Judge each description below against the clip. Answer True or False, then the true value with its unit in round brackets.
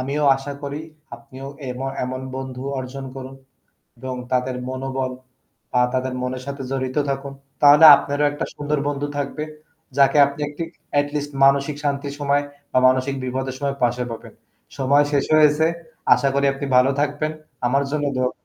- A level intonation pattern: True (1.8 semitones)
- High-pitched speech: False (140 Hz)